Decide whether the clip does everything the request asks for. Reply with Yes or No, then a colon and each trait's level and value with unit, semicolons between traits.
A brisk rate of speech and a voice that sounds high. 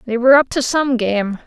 Yes: fast, 245 wpm; high, 245 Hz